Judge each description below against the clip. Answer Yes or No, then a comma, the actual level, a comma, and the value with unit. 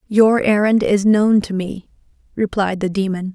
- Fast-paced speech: No, average, 160 wpm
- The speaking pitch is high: Yes, high, 200 Hz